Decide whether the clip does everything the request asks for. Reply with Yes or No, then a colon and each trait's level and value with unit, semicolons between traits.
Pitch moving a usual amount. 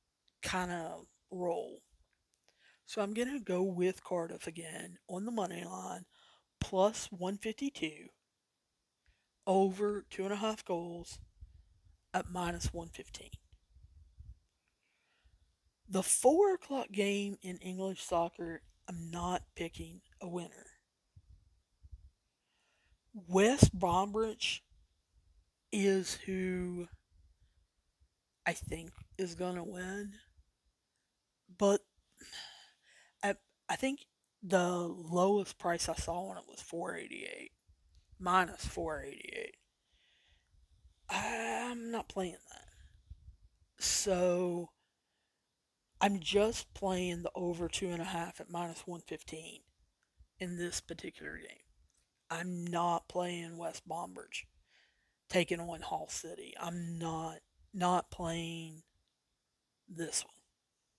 Yes: average, 3.5 semitones